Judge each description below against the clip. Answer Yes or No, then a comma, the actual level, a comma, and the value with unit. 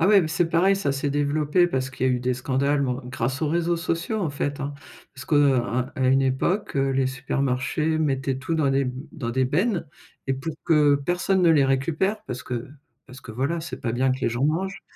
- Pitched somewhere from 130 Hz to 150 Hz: Yes, medium, 140 Hz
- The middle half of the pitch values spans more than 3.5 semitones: Yes, average, 3.9 semitones